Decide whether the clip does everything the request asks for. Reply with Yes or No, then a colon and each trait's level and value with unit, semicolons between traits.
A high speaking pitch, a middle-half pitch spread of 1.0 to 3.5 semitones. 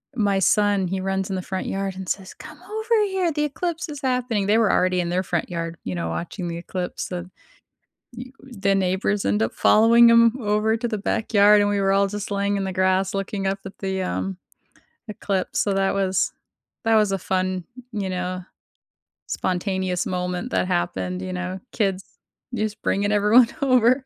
Yes: high, 195 Hz; average, 2.7 semitones